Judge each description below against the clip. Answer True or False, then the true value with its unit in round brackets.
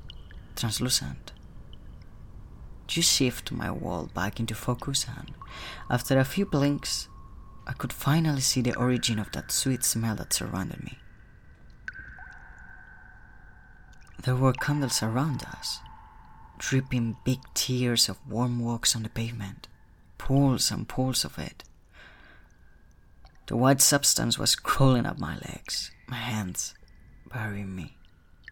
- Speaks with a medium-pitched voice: False (120 Hz)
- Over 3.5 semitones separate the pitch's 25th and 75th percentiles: True (4.5 semitones)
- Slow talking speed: True (120 wpm)